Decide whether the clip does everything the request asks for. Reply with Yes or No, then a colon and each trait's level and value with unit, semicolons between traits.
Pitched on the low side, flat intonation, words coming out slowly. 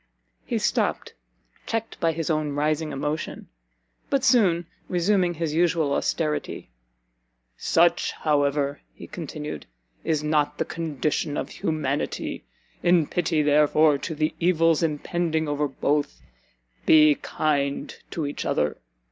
No: medium, 155 Hz; narrow, 2.3 semitones; slow, 120 wpm